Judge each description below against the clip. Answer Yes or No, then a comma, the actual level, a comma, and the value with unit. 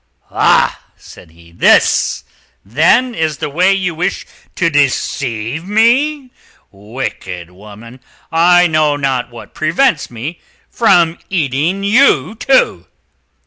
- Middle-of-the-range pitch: Yes, medium, 155 Hz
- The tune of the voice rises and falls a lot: Yes, wide, 7.8 semitones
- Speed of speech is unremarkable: No, slow, 110 wpm